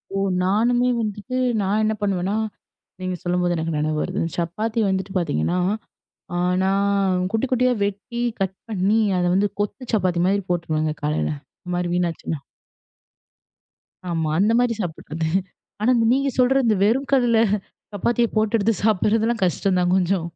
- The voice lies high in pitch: Yes, high, 195 Hz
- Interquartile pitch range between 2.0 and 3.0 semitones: No, average, 4.0 semitones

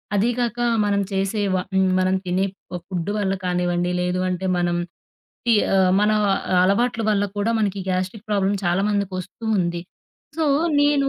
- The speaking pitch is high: Yes, high, 195 Hz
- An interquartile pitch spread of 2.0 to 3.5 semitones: Yes, narrow, 2.4 semitones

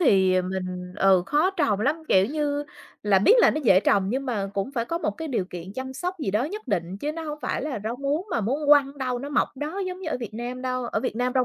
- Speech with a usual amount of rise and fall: No, wide, 6.9 semitones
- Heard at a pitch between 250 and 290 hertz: Yes, very high, 255 Hz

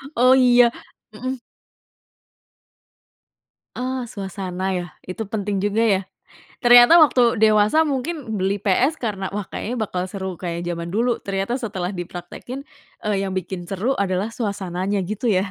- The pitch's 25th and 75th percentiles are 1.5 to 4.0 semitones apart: No, average, 4.4 semitones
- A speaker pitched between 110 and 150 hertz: No, high, 205 Hz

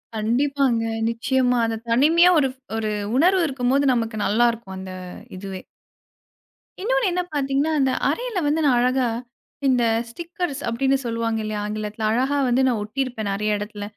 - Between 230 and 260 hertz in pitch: Yes, high, 245 Hz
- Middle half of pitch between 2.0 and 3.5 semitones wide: No, average, 4.4 semitones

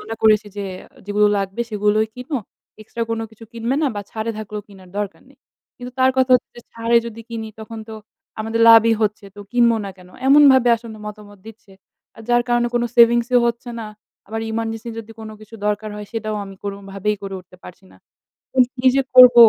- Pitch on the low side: No, high, 225 Hz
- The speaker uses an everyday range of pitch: No, narrow, 2.2 semitones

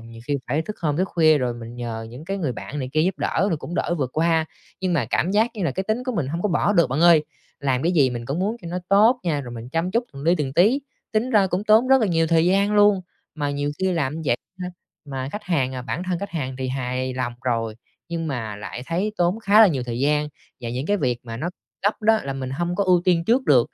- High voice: No, medium, 160 Hz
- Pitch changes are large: Yes, wide, 6.5 semitones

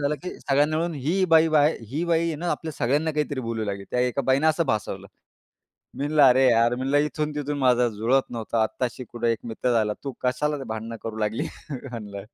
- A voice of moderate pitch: No, low, 130 Hz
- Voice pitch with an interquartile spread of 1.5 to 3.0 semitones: No, average, 4.8 semitones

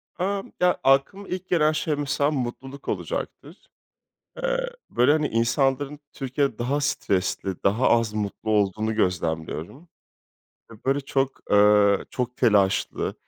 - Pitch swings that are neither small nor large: No, wide, 5.7 semitones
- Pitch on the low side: Yes, low, 130 Hz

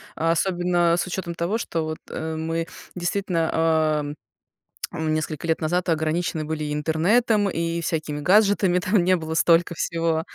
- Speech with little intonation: Yes, narrow, 2.0 semitones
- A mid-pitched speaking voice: Yes, medium, 165 Hz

